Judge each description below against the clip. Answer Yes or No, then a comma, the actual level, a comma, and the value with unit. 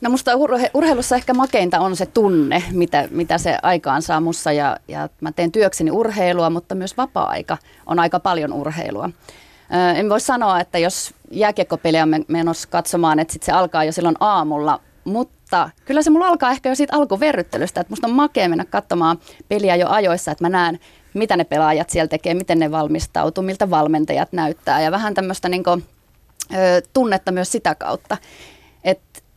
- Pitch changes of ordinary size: Yes, average, 4.3 semitones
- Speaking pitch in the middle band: Yes, medium, 180 Hz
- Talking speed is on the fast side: Yes, fast, 175 wpm